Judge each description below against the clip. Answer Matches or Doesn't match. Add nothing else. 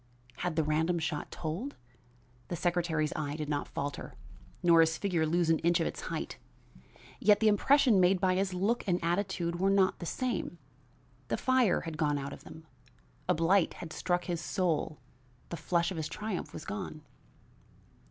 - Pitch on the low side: Doesn't match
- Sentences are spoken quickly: Doesn't match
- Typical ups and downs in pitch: Matches